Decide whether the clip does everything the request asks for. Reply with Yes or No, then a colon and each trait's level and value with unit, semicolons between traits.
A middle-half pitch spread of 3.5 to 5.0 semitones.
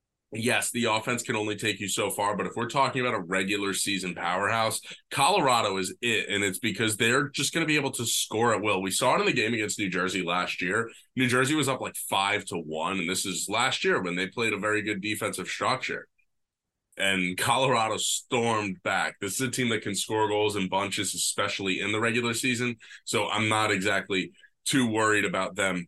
Yes: average, 3.8 semitones